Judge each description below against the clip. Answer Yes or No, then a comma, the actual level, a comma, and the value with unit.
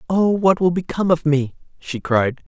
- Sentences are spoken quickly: No, average, 190 wpm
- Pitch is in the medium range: Yes, medium, 165 Hz